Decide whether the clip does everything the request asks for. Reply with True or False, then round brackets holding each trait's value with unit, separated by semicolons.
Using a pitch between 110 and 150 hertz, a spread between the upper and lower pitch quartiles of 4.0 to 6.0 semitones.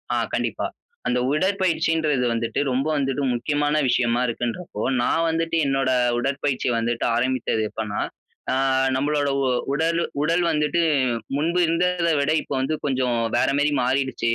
True (140 Hz; 4.4 semitones)